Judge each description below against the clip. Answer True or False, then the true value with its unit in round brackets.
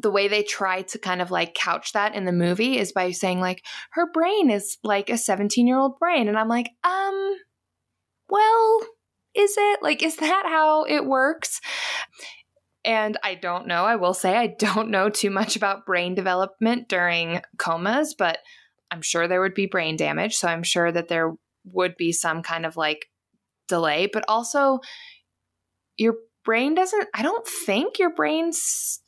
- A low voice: False (215 Hz)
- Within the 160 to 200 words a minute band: True (175 wpm)